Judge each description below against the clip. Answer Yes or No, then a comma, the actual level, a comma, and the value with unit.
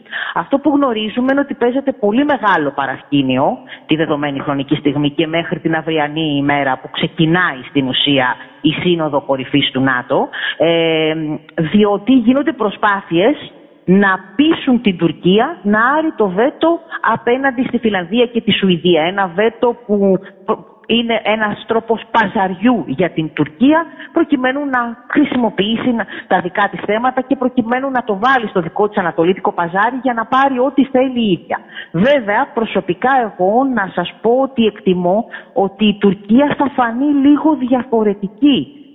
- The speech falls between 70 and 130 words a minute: No, average, 145 wpm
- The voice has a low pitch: No, high, 210 Hz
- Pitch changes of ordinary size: No, wide, 6.8 semitones